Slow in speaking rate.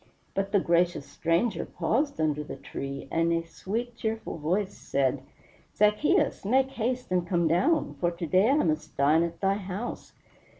No: average, 165 wpm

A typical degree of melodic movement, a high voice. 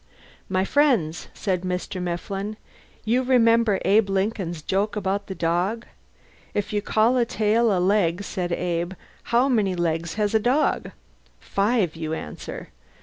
Yes: average, 3.8 semitones; high, 200 Hz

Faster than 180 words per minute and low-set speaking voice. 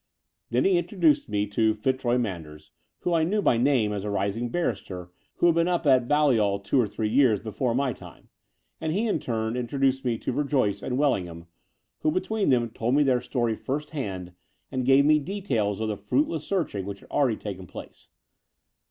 Yes: average, 195 wpm; low, 125 Hz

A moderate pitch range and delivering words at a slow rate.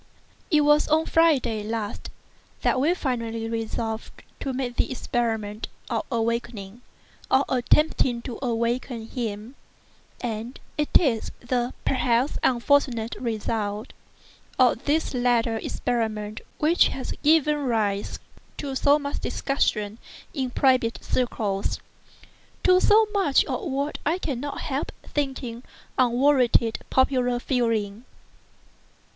Yes: average, 3.6 semitones; slow, 110 wpm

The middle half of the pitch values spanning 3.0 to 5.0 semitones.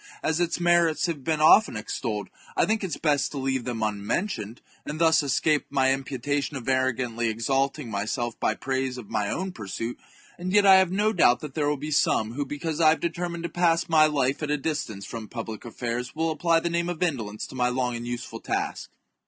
No: wide, 5.5 semitones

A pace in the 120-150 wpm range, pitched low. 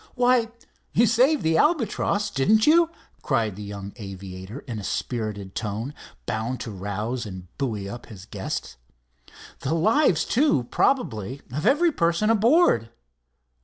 Yes: slow, 135 wpm; low, 130 Hz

